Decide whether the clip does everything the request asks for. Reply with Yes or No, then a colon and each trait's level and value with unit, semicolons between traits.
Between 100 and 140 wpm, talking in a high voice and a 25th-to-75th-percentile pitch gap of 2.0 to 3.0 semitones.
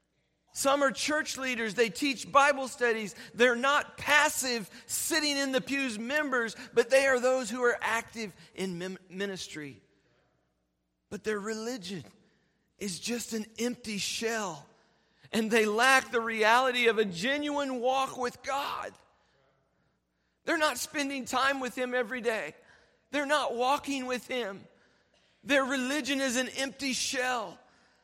No: slow, 135 wpm; high, 245 Hz; average, 3.8 semitones